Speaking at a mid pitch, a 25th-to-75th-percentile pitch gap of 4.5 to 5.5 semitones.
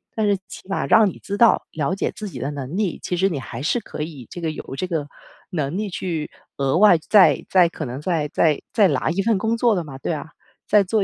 Yes: medium, 175 Hz; average, 5.2 semitones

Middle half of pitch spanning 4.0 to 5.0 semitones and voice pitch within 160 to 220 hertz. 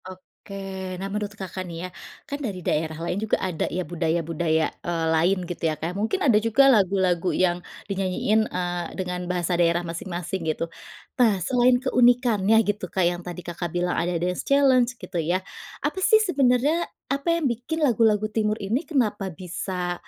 Yes: average, 4.6 semitones; high, 190 Hz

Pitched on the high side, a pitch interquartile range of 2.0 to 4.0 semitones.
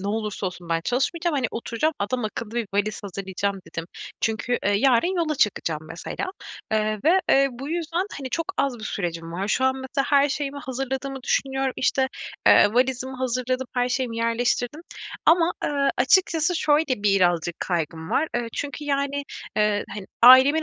No: very high, 250 Hz; average, 5.1 semitones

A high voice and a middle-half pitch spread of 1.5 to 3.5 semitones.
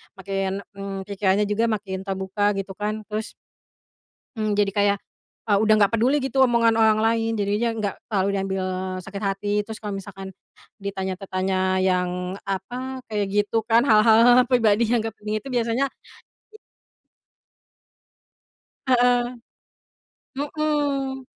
Yes: high, 210 Hz; average, 3.1 semitones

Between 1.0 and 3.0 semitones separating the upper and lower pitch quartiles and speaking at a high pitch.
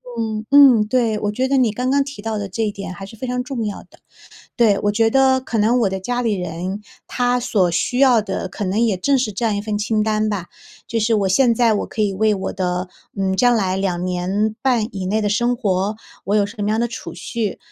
No: average, 3.4 semitones; high, 215 Hz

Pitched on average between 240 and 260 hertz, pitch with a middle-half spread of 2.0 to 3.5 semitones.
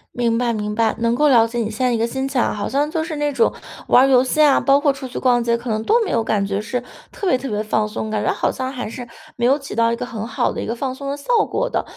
Yes: high, 245 Hz; average, 3.2 semitones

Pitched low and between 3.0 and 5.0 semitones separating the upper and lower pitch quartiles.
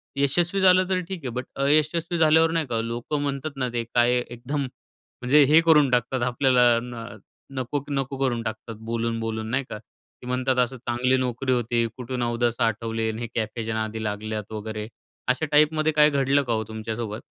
Yes: low, 125 Hz; average, 3.7 semitones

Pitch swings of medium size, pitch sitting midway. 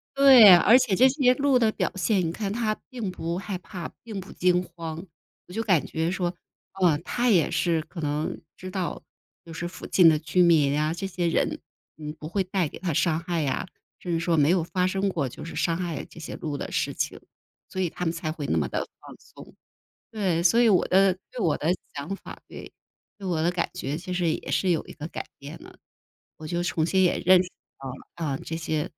Yes: average, 3.0 semitones; medium, 175 Hz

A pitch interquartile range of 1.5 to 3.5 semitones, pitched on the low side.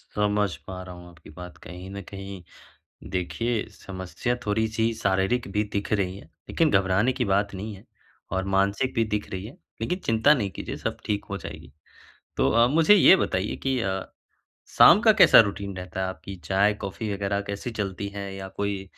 Yes: average, 2.8 semitones; low, 100 Hz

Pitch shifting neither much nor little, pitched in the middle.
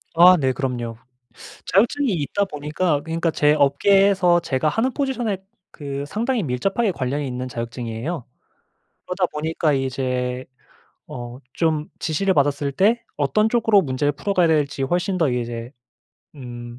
No: wide, 6.4 semitones; medium, 150 Hz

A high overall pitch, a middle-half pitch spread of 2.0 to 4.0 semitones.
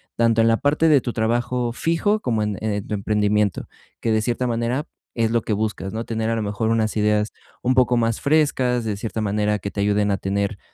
No: low, 110 Hz; narrow, 2.4 semitones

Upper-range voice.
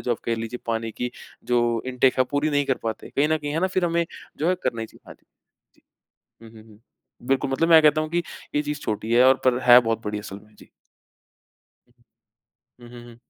No: low, 125 Hz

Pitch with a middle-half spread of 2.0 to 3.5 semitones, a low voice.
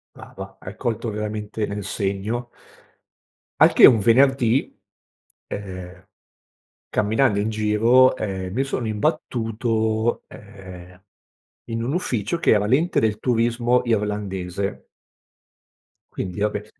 Yes: average, 2.7 semitones; low, 110 Hz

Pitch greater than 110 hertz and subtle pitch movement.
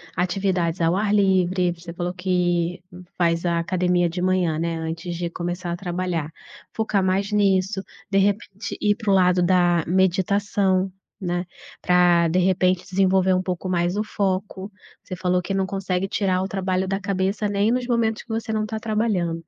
Yes: medium, 185 Hz; narrow, 1.9 semitones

